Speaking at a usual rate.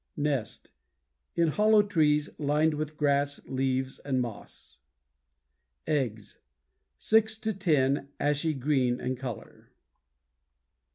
No: slow, 100 wpm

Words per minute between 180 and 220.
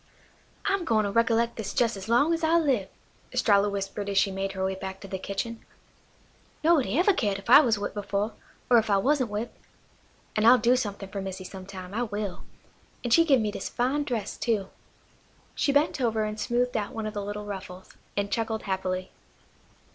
Yes: average, 200 wpm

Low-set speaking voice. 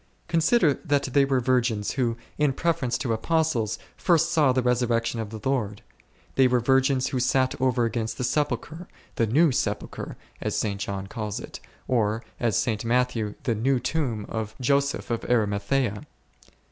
Yes: low, 125 Hz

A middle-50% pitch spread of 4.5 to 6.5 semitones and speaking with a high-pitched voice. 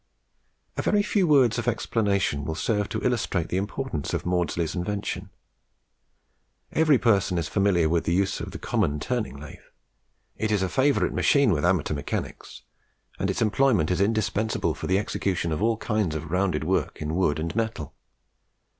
No: average, 5.0 semitones; low, 100 Hz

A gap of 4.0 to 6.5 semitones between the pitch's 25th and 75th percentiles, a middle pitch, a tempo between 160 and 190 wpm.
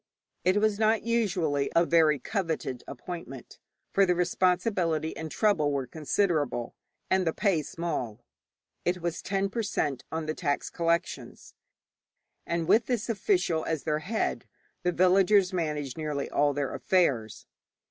No: average, 4.4 semitones; medium, 170 Hz; average, 140 wpm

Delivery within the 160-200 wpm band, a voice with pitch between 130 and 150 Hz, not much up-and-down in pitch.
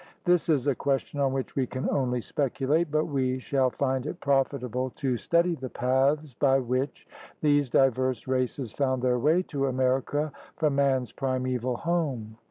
Yes: average, 165 wpm; low, 135 Hz; narrow, 2.2 semitones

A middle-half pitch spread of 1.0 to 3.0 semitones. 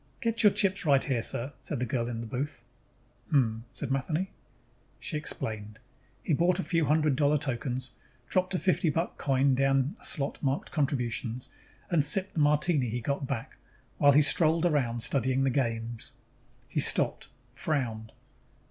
No: average, 3.9 semitones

